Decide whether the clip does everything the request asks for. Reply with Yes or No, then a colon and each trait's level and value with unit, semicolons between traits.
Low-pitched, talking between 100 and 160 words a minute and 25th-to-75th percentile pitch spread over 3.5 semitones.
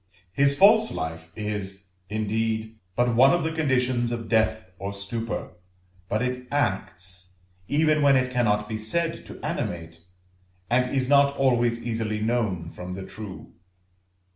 Yes: low, 115 Hz; average, 140 wpm; average, 4.2 semitones